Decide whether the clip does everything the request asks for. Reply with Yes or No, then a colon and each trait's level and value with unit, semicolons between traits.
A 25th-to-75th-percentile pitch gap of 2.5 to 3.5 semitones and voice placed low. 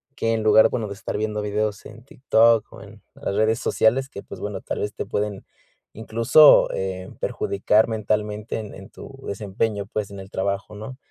No: narrow, 1.8 semitones; low, 105 Hz